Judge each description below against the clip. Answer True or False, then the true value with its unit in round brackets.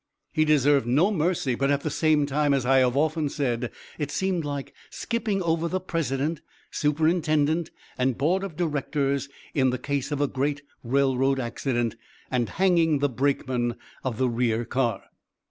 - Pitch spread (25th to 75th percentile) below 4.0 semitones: True (3.3 semitones)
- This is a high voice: False (140 Hz)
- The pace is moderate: True (165 wpm)